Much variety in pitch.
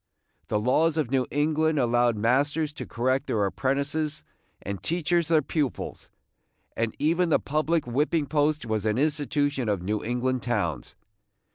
No: average, 4.6 semitones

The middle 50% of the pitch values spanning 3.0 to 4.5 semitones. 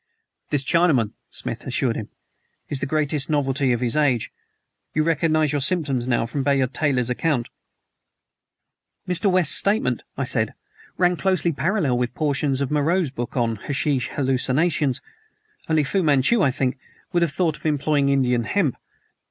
Yes: average, 3.7 semitones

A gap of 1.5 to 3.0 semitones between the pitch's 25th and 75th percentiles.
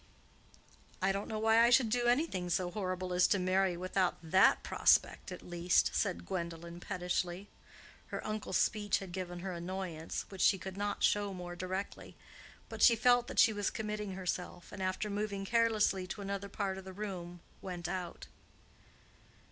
Yes: narrow, 2.5 semitones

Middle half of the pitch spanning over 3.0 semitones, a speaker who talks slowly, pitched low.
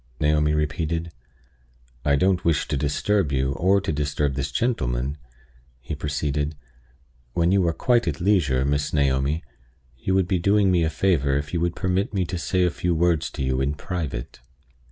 No: average, 4.2 semitones; average, 175 wpm; very low, 80 Hz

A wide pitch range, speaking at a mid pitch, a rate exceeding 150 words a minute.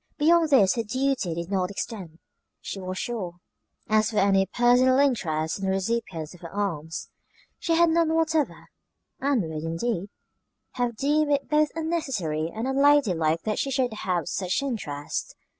No: wide, 7.6 semitones; high, 220 Hz; average, 160 wpm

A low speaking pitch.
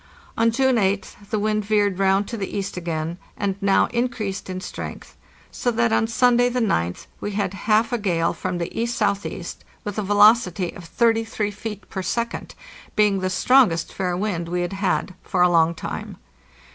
No: high, 200 Hz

